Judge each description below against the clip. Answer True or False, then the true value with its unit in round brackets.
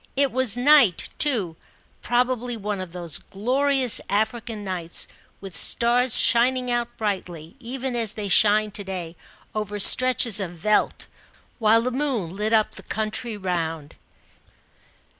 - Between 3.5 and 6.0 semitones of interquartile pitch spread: True (4.2 semitones)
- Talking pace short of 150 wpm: True (135 wpm)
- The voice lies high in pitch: True (215 Hz)